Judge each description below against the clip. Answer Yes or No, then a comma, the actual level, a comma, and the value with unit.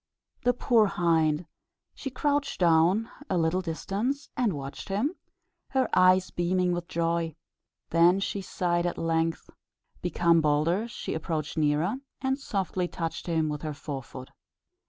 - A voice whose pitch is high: No, medium, 175 Hz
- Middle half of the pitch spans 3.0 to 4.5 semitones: Yes, average, 3.6 semitones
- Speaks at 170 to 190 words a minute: No, average, 145 wpm